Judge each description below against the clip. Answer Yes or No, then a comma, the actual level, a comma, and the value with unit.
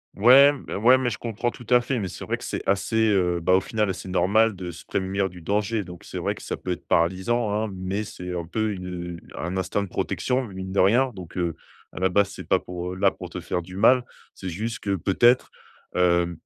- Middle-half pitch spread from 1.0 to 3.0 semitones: No, average, 3.5 semitones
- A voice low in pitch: Yes, very low, 95 Hz